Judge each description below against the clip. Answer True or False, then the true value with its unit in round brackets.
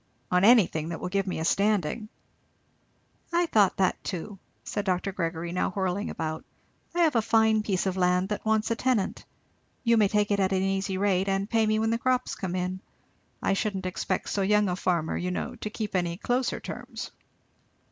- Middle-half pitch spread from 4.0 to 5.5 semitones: False (3.0 semitones)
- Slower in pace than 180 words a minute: False (200 wpm)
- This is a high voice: True (195 Hz)